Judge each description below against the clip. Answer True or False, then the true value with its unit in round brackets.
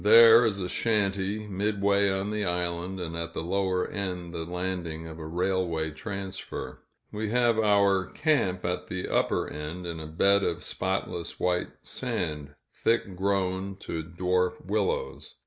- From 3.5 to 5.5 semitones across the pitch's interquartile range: False (2.8 semitones)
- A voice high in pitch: False (95 Hz)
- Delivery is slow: False (150 wpm)